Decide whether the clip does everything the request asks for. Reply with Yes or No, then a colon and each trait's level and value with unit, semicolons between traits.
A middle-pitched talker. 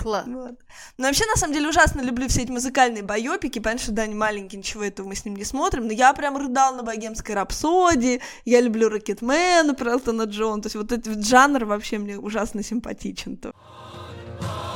No: high, 230 Hz